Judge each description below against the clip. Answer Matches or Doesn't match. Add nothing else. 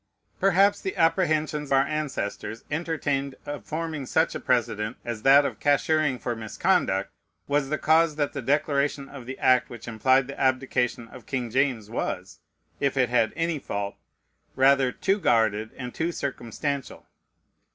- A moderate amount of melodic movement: Matches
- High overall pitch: Doesn't match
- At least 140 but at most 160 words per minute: Matches